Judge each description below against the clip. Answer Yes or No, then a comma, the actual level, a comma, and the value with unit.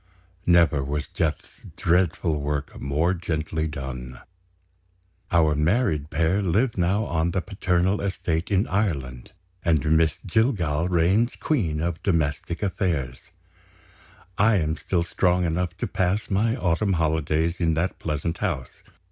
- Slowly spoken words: Yes, slow, 130 wpm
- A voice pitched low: Yes, very low, 85 Hz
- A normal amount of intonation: Yes, average, 3.5 semitones